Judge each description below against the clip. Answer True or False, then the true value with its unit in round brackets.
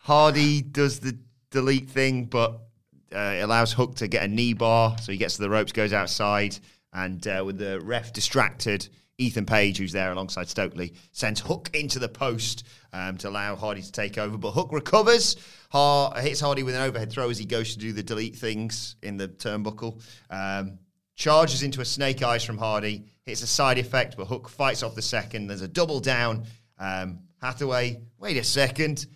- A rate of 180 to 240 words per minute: True (195 wpm)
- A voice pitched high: False (115 Hz)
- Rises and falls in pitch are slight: False (4.3 semitones)